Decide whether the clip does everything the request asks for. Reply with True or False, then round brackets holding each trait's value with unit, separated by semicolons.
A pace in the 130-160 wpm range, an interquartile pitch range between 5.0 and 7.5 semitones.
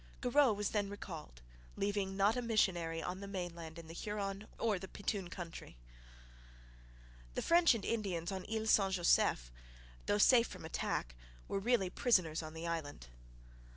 False (155 wpm; 3.9 semitones)